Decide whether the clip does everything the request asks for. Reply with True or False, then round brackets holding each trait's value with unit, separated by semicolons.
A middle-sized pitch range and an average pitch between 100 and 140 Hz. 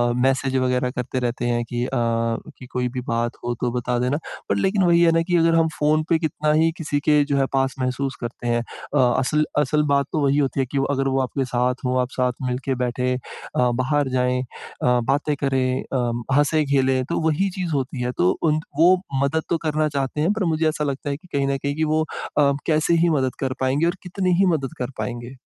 True (3.3 semitones; 135 Hz)